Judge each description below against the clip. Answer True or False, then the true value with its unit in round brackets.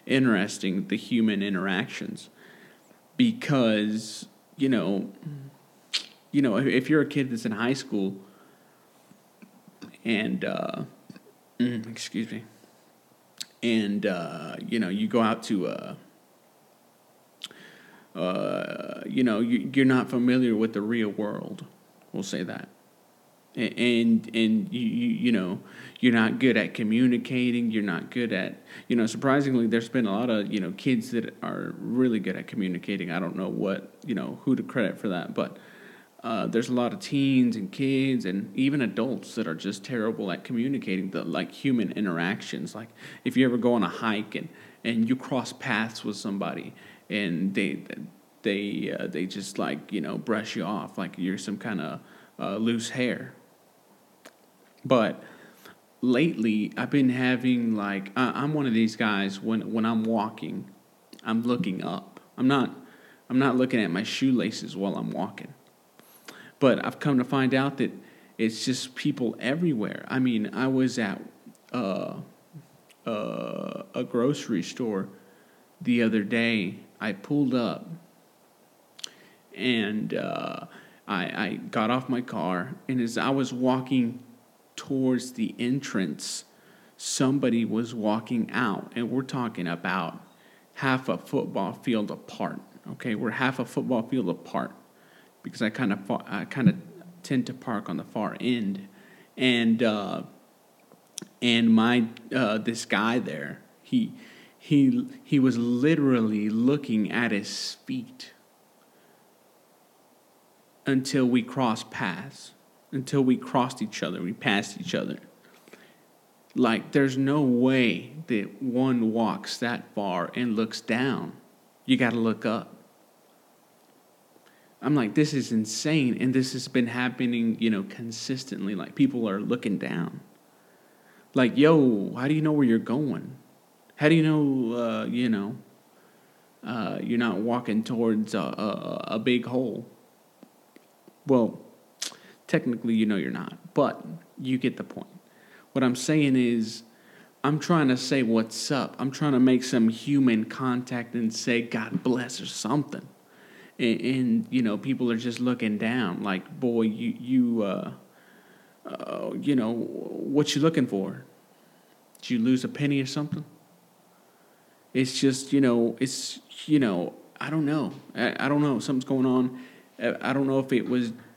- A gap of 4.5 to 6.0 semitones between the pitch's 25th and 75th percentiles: False (3.3 semitones)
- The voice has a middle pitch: False (125 Hz)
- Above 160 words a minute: False (150 wpm)